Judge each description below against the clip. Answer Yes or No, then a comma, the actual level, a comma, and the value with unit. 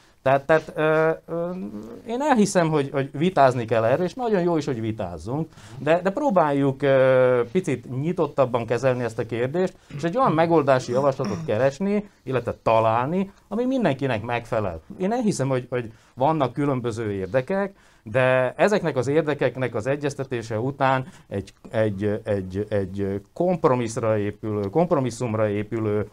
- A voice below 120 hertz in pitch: No, low, 135 Hz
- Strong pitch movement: Yes, wide, 6.3 semitones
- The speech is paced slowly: No, average, 135 wpm